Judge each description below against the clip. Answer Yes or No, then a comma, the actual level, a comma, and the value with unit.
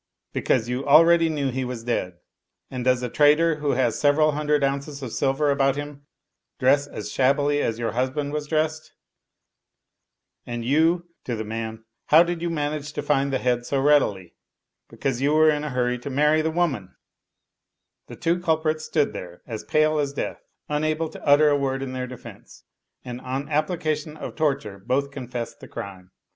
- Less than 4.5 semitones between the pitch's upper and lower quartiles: Yes, average, 3.3 semitones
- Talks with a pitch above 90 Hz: Yes, medium, 140 Hz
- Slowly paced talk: No, average, 185 wpm